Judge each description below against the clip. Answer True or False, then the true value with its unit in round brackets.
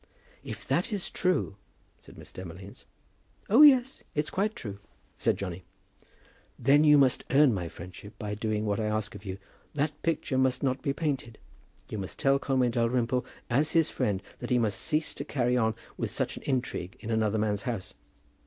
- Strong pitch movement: True (5.7 semitones)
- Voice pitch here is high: False (120 Hz)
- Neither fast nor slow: True (180 wpm)